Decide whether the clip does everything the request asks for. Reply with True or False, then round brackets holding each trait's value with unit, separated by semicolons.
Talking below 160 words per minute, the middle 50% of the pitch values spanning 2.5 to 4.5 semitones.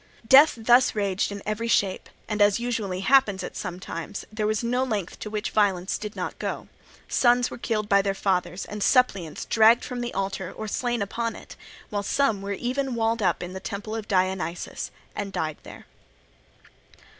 False (185 wpm; 3.2 semitones)